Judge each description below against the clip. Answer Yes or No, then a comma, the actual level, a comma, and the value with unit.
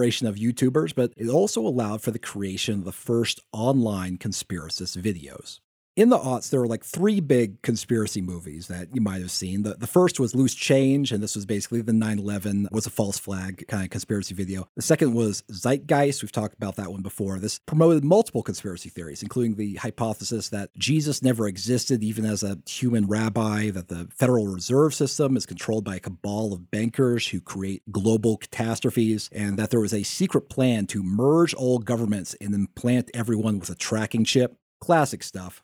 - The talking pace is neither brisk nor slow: Yes, average, 190 wpm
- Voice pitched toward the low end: Yes, low, 110 Hz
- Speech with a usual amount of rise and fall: Yes, average, 3.8 semitones